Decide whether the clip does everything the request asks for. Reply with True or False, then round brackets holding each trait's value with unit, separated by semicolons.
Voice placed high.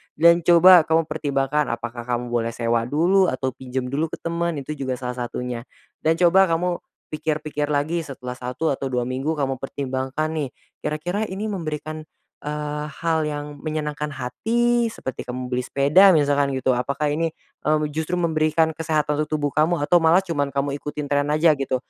False (150 Hz)